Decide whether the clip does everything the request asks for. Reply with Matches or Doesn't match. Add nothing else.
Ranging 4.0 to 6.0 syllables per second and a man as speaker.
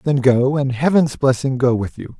Matches